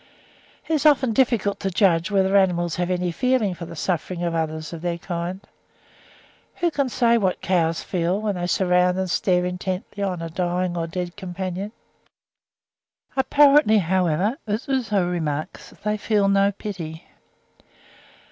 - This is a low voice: No, medium, 185 Hz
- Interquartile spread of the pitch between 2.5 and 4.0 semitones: Yes, average, 3.2 semitones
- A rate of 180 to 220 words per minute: No, average, 150 wpm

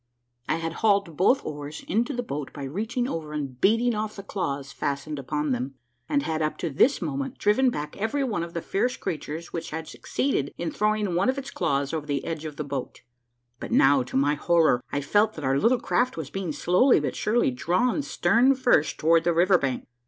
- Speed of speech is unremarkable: No, fast, 210 wpm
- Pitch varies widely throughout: Yes, wide, 6.9 semitones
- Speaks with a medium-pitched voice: Yes, medium, 165 Hz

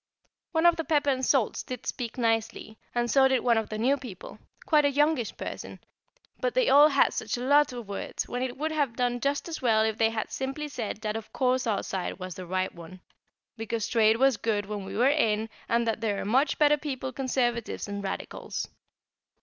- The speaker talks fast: Yes, fast, 215 wpm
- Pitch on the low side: No, high, 240 Hz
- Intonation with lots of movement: No, average, 4.1 semitones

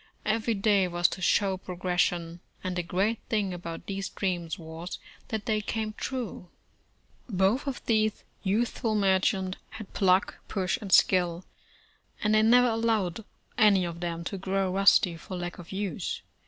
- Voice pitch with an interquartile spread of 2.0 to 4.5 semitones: Yes, average, 3.3 semitones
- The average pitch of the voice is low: No, high, 195 Hz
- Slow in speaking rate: No, average, 155 wpm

